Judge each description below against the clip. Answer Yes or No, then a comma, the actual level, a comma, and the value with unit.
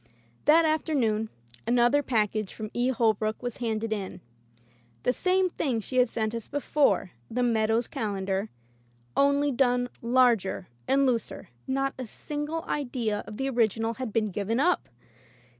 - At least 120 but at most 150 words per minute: Yes, average, 140 wpm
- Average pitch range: Yes, average, 3.8 semitones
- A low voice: No, high, 240 Hz